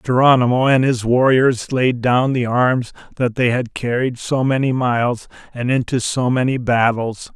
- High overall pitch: No, low, 125 Hz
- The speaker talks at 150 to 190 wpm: Yes, average, 165 wpm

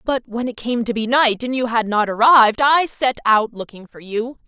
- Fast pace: Yes, fast, 240 wpm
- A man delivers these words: No, female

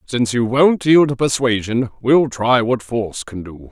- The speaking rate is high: No, average, 195 wpm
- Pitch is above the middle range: No, low, 120 Hz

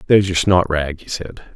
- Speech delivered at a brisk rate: No, average, 195 wpm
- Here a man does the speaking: Yes, male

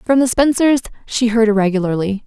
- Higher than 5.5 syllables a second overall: Yes, 5.7 syllables/s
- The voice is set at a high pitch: Yes, high, 230 Hz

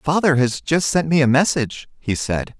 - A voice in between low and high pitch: Yes, medium, 145 Hz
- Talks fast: Yes, fast, 210 wpm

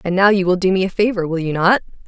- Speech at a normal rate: No, fast, 320 wpm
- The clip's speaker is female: Yes, female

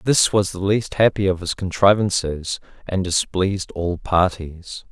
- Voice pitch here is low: Yes, very low, 95 Hz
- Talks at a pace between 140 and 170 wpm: Yes, average, 145 wpm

